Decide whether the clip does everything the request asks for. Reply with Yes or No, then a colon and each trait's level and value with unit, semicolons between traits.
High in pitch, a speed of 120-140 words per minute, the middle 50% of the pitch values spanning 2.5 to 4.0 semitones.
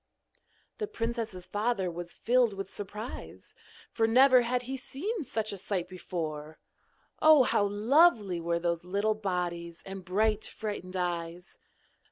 No: high, 205 Hz; slow, 135 wpm; average, 5.0 semitones